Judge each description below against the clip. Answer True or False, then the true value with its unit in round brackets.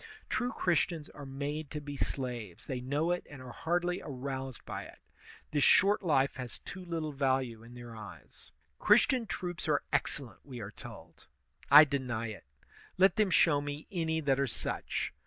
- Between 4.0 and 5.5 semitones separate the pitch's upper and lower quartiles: True (4.4 semitones)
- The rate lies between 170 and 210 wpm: True (175 wpm)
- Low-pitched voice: False (145 Hz)